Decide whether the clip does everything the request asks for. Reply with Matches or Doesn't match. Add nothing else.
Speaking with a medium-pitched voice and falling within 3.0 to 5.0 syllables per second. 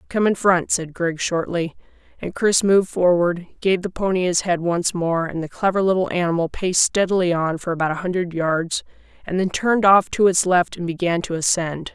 Doesn't match